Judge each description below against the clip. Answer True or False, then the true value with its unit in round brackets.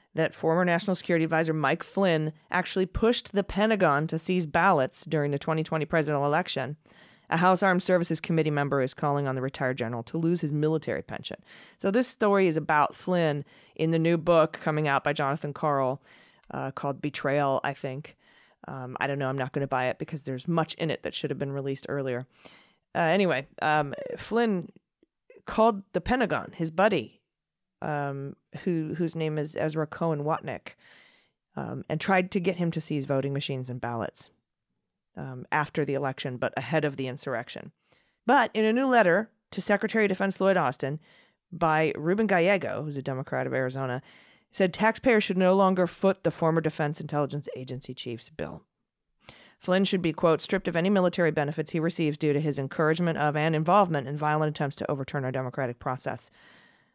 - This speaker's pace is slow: False (180 wpm)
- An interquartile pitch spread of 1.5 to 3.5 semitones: False (4.4 semitones)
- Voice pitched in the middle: True (155 Hz)